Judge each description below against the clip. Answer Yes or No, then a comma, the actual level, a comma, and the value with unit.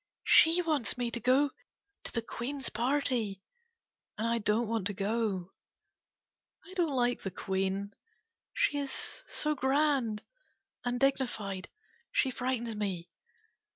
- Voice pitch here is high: Yes, high, 235 Hz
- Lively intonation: No, average, 4.8 semitones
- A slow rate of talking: Yes, slow, 130 wpm